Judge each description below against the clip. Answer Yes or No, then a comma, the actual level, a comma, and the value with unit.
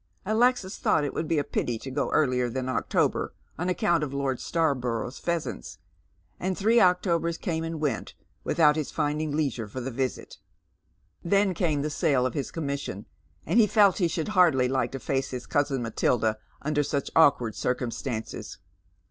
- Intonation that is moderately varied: Yes, average, 4.7 semitones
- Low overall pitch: No, medium, 145 Hz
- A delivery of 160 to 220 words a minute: Yes, average, 170 wpm